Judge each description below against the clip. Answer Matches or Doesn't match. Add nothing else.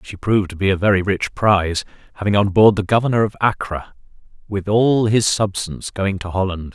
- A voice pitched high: Doesn't match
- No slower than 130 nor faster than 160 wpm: Doesn't match